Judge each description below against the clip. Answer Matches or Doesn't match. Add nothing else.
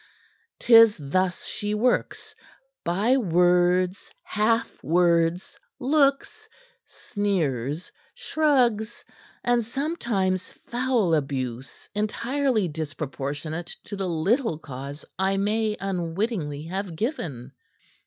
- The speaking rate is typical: Doesn't match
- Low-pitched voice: Doesn't match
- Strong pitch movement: Matches